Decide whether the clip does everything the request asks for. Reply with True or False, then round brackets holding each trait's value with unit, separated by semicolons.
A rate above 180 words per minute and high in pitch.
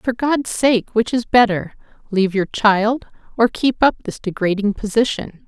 False (165 wpm; 220 Hz)